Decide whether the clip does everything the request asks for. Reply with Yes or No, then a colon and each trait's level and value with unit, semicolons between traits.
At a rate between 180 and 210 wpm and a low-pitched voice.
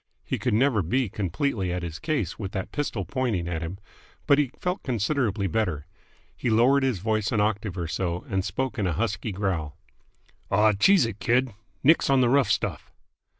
Yes: average, 190 wpm; low, 105 Hz